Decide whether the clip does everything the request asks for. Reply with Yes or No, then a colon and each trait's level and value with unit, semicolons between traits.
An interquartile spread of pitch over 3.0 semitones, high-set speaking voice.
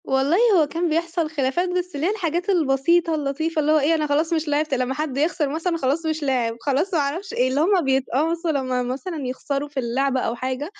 Yes: average, 3.7 semitones; very high, 300 Hz